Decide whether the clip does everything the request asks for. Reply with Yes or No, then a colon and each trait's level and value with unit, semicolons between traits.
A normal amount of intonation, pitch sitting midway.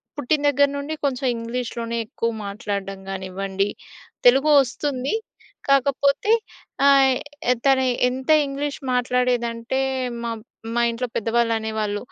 No: average, 3.2 semitones; very high, 250 Hz